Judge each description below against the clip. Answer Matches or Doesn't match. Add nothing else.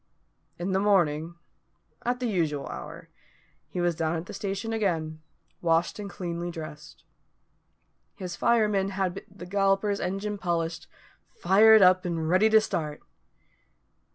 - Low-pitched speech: Doesn't match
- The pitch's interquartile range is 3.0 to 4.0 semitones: Matches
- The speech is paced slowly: Matches